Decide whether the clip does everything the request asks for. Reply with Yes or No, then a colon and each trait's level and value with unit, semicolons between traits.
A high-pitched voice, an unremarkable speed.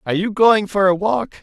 No: high, 195 Hz; fast, 255 wpm